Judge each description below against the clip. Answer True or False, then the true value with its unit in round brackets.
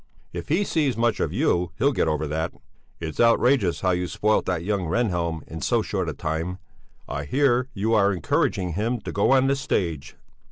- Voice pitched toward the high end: False (95 Hz)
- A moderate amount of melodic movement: False (6.1 semitones)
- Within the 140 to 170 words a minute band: False (195 wpm)